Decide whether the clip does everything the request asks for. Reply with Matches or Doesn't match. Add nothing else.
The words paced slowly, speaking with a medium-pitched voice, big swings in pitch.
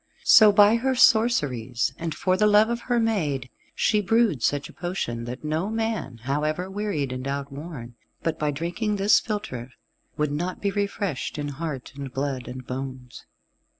Doesn't match